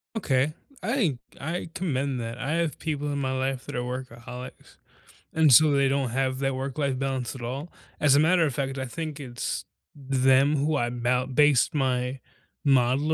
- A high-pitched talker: No, low, 135 Hz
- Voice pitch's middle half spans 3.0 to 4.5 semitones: No, narrow, 2.5 semitones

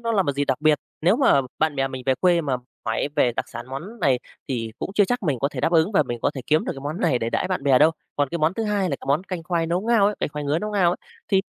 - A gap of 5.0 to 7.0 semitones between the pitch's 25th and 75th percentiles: Yes, wide, 5.6 semitones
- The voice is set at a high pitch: No, medium, 155 Hz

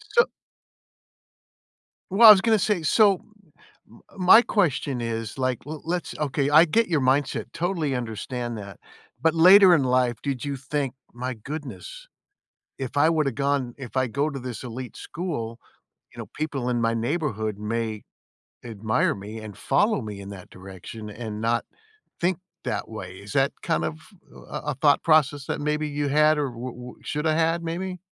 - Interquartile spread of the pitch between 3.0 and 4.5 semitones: No, wide, 5.6 semitones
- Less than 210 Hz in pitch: Yes, low, 135 Hz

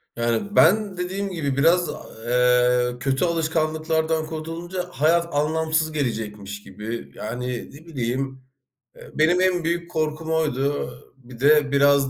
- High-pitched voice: No, medium, 155 Hz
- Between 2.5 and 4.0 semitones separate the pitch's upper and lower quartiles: No, average, 4.5 semitones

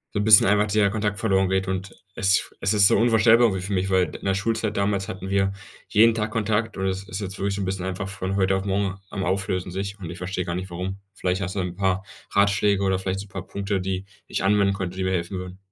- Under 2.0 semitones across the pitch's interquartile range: Yes, narrow, 1.3 semitones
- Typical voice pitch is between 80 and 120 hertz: Yes, very low, 95 Hz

